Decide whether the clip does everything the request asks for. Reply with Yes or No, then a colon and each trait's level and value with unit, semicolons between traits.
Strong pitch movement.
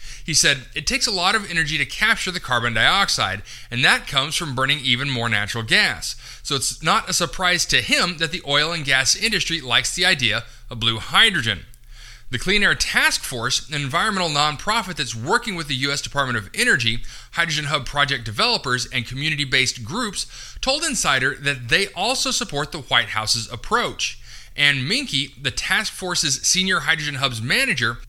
Yes: wide, 5.9 semitones